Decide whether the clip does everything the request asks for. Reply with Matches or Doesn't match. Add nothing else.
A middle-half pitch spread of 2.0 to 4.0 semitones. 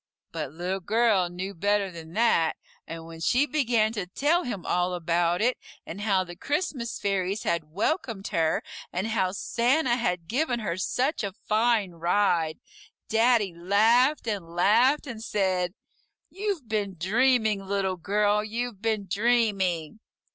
Doesn't match